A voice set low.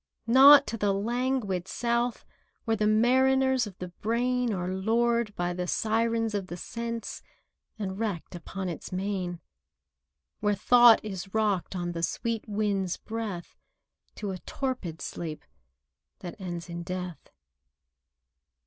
No: high, 210 Hz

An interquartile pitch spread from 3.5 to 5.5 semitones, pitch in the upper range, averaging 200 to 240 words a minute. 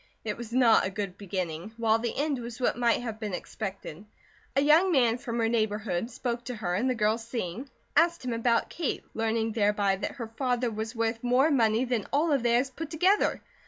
No: average, 2.8 semitones; high, 230 Hz; fast, 205 wpm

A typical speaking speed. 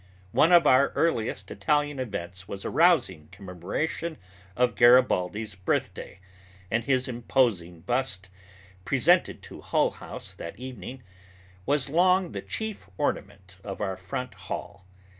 No: slow, 125 wpm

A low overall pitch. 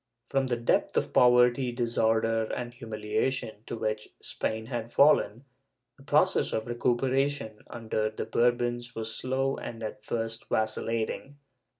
Yes: low, 120 Hz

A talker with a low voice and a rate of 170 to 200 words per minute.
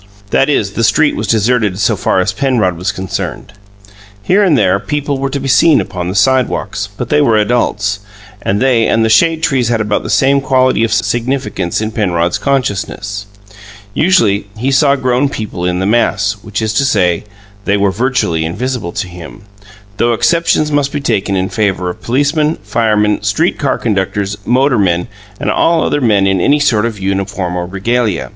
Yes: low, 110 Hz; average, 180 wpm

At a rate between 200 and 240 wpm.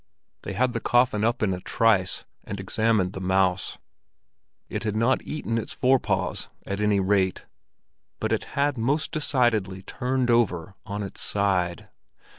No: average, 150 wpm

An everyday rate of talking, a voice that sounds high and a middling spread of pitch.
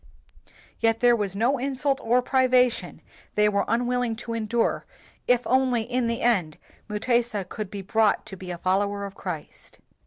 Yes: average, 160 wpm; high, 230 Hz; average, 3.5 semitones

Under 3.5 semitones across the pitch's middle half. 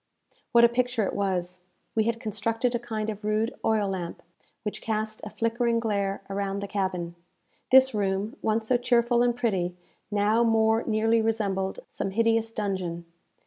Yes: average, 2.7 semitones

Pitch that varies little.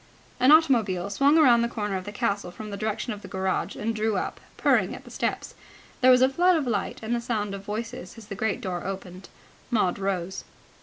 No: average, 3.6 semitones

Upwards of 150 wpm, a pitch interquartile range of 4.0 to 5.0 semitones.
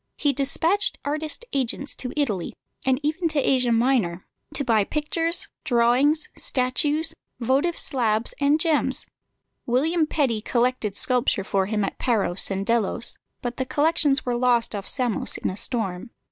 No: average, 145 wpm; average, 4.5 semitones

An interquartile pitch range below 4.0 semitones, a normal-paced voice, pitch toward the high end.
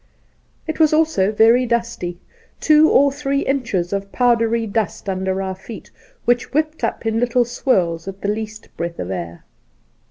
No: average, 5.1 semitones; average, 165 wpm; high, 225 Hz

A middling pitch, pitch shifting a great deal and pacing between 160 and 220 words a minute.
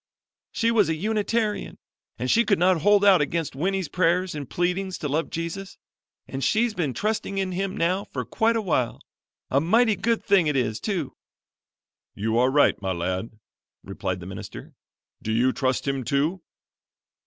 Yes: medium, 170 Hz; wide, 7.0 semitones; average, 165 wpm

